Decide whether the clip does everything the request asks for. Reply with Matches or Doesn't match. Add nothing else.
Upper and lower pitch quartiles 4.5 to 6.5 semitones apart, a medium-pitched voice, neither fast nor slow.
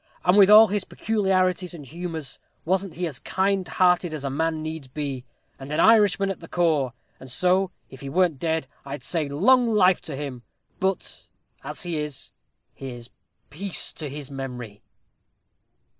Matches